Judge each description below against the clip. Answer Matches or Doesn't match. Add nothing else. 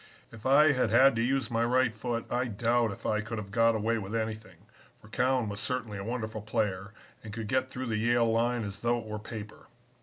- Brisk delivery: Matches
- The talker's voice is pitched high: Doesn't match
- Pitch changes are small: Matches